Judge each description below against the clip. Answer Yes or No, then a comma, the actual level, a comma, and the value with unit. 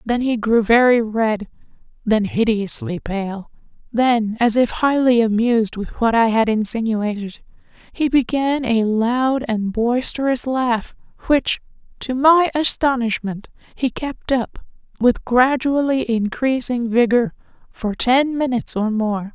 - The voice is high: Yes, high, 235 Hz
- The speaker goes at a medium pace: No, slow, 120 wpm